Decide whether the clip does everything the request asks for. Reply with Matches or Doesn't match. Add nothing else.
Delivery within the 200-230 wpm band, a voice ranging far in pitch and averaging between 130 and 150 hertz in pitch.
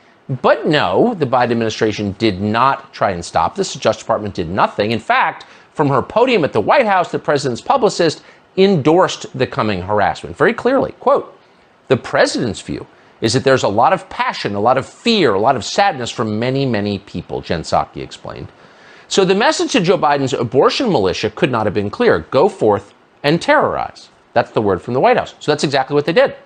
Matches